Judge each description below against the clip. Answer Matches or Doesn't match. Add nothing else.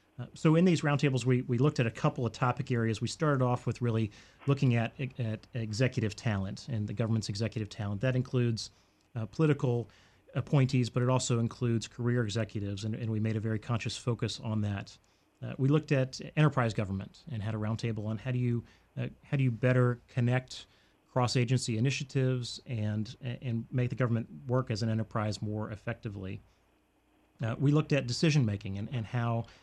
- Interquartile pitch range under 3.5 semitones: Matches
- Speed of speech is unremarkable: Matches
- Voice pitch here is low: Matches